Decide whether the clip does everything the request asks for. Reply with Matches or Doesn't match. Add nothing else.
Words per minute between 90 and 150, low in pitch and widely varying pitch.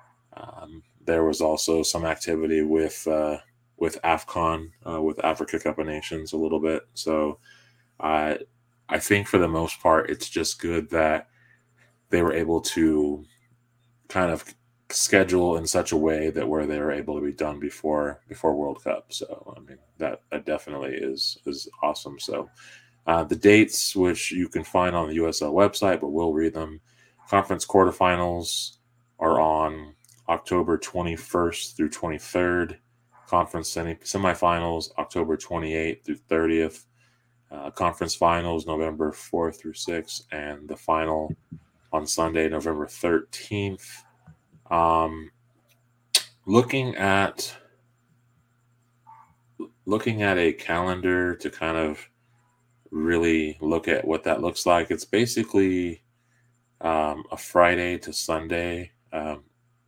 Matches